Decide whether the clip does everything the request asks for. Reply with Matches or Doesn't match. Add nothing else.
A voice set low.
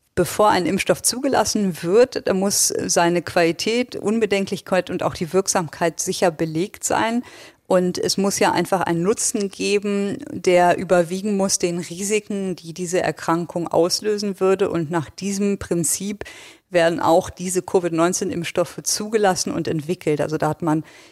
Doesn't match